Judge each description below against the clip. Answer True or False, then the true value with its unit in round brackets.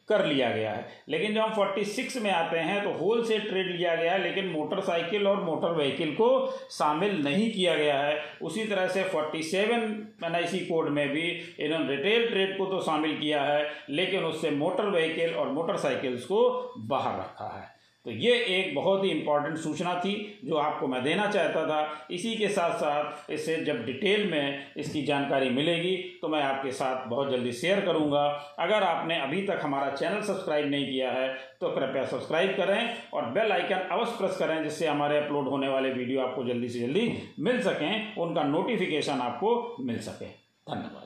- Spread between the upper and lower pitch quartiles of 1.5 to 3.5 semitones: False (5.1 semitones)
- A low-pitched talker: False (165 Hz)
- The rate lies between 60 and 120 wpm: False (190 wpm)